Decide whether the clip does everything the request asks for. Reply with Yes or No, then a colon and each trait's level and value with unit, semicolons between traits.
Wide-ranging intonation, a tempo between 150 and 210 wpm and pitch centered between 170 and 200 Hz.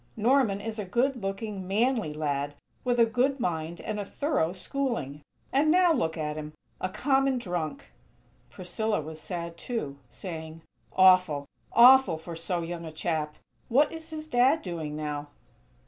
Yes: wide, 7.6 semitones; average, 155 wpm; medium, 185 Hz